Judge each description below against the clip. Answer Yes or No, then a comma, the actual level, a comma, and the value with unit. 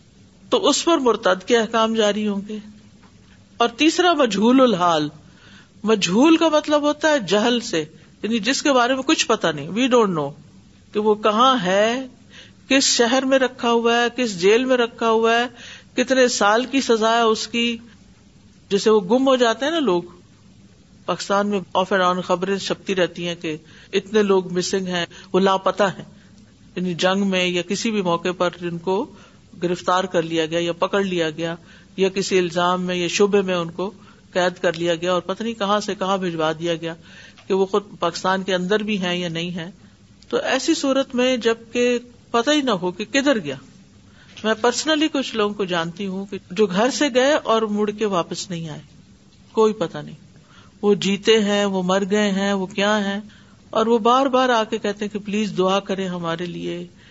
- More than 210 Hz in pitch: No, high, 205 Hz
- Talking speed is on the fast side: Yes, fast, 195 wpm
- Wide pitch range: No, average, 4.6 semitones